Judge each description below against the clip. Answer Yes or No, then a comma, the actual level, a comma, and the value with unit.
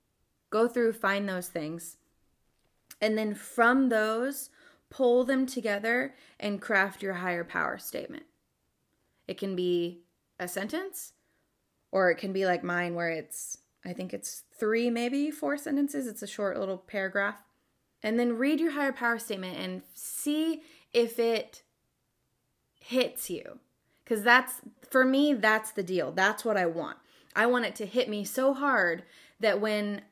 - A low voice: No, high, 220 Hz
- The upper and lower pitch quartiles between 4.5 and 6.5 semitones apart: Yes, average, 5.2 semitones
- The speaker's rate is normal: Yes, average, 155 wpm